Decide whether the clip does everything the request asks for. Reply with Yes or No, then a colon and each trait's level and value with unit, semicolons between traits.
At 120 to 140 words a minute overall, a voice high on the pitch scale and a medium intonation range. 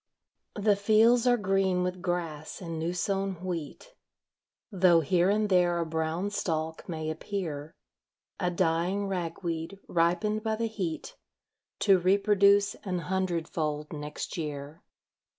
No: slow, 135 wpm; medium, 180 Hz; average, 3.5 semitones